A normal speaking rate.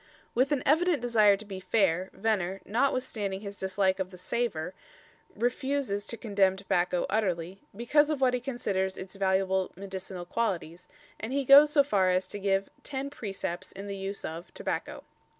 Yes: average, 170 wpm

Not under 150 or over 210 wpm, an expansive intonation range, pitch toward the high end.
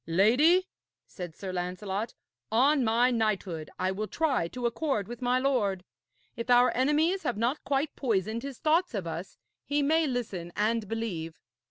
Yes: average, 160 wpm; wide, 5.9 semitones; high, 230 Hz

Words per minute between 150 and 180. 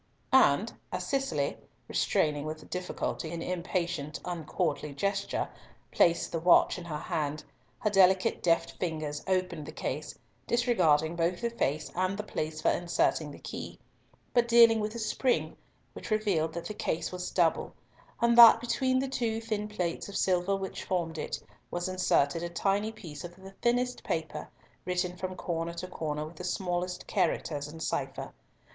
Yes: average, 165 wpm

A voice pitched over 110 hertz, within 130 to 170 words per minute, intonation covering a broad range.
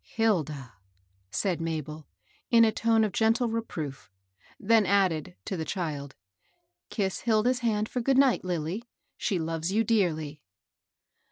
Yes: high, 190 Hz; average, 155 wpm; wide, 6.3 semitones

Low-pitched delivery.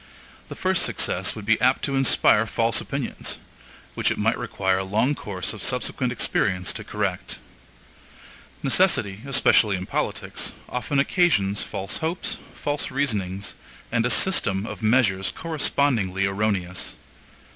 Yes: low, 110 Hz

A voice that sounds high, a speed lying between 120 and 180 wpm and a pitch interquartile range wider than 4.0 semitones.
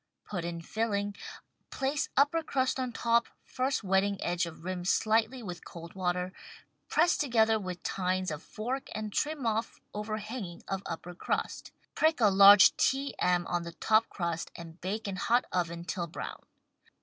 Yes: high, 200 Hz; average, 160 wpm; average, 4.8 semitones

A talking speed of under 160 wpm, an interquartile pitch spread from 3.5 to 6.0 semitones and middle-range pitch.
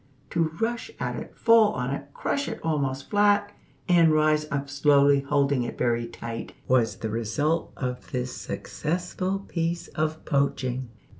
Yes: average, 150 wpm; average, 4.6 semitones; medium, 145 Hz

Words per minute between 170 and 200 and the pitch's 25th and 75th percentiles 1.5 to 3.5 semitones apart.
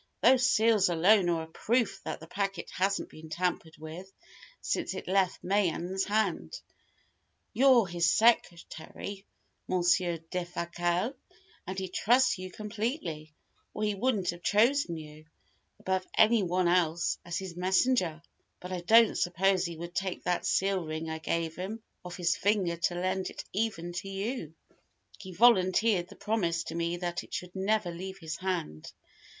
No: average, 155 wpm; average, 3.1 semitones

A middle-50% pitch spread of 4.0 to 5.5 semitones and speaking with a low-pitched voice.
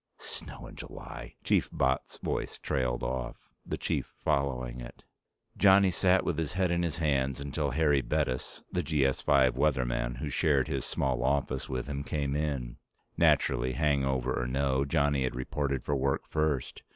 No: average, 2.8 semitones; very low, 70 Hz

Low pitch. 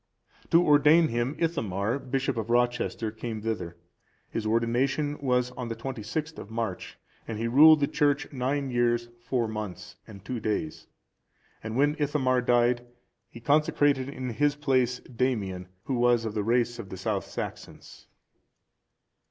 Yes: low, 120 Hz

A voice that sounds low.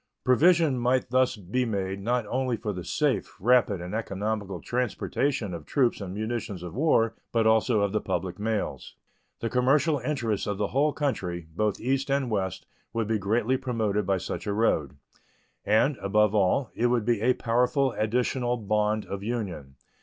Yes: low, 110 Hz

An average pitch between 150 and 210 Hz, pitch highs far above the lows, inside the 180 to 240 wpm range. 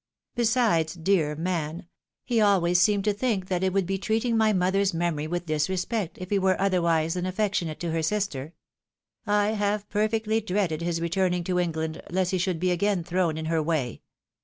No: medium, 185 Hz; average, 3.5 semitones; average, 185 wpm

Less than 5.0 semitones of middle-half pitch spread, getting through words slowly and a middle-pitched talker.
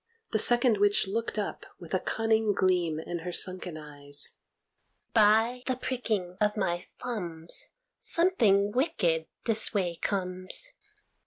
No: average, 4.3 semitones; slow, 130 wpm; high, 205 Hz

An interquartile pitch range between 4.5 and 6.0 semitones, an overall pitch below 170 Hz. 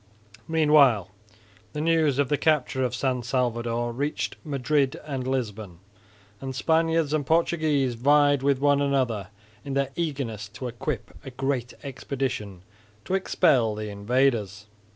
No: average, 3.7 semitones; low, 135 Hz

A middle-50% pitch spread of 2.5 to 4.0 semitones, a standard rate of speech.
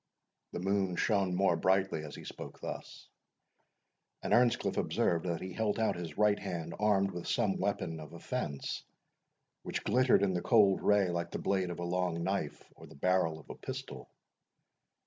Yes: average, 2.9 semitones; average, 175 wpm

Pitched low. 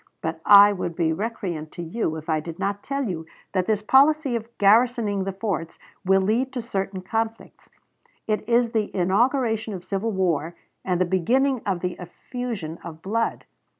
No: high, 200 Hz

